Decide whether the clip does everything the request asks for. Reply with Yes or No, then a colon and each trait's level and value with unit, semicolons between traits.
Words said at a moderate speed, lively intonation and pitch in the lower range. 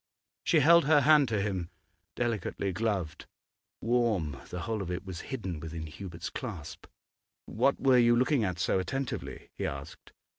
Yes: average, 155 wpm; wide, 6.2 semitones; low, 105 Hz